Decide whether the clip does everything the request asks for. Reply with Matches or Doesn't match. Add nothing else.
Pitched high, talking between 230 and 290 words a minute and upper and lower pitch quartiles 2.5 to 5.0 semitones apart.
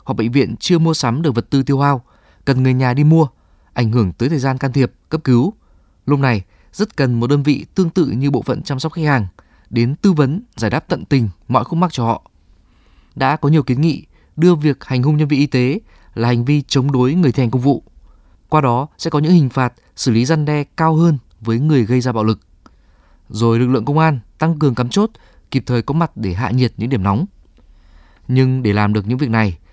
Doesn't match